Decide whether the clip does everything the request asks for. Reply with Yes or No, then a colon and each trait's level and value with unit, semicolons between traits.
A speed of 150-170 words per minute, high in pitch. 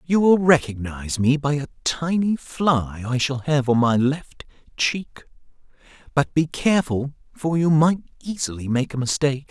No: average, 160 wpm; medium, 145 Hz